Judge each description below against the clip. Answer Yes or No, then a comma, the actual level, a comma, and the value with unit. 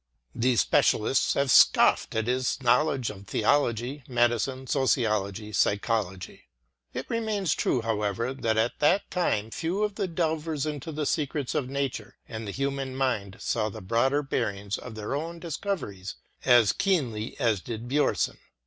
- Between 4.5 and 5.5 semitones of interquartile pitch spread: Yes, average, 5.0 semitones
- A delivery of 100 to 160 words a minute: Yes, average, 150 wpm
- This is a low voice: Yes, low, 125 Hz